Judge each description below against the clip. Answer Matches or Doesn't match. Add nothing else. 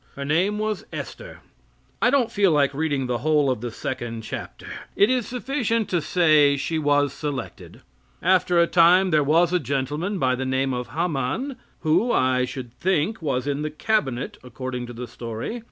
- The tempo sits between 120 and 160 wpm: Doesn't match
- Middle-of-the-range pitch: Matches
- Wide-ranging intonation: Matches